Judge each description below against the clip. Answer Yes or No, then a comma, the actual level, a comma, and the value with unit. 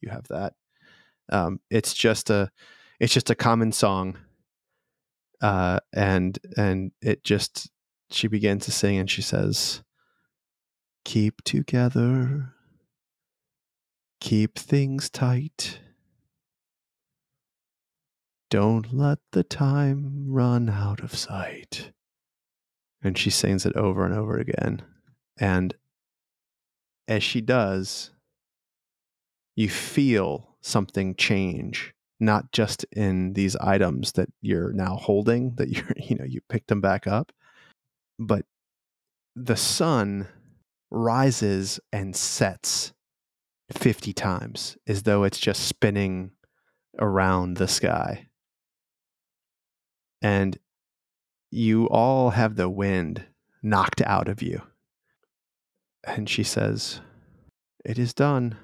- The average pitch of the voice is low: Yes, low, 105 Hz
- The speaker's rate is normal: No, slow, 105 wpm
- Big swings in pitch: No, average, 4.3 semitones